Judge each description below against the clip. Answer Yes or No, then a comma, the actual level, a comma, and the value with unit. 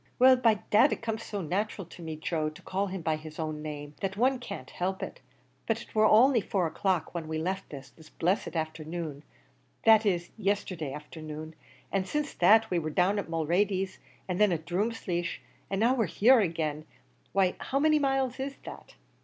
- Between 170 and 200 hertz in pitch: Yes, medium, 185 Hz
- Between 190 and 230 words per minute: Yes, average, 195 wpm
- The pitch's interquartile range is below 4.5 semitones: No, wide, 5.6 semitones